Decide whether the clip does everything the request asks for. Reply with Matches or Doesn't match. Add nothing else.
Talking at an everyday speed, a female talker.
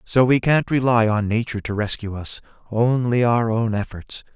Doesn't match